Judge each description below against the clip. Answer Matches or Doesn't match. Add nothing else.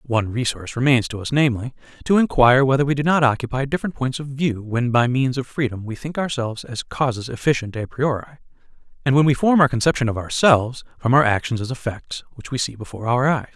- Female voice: Doesn't match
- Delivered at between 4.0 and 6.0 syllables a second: Doesn't match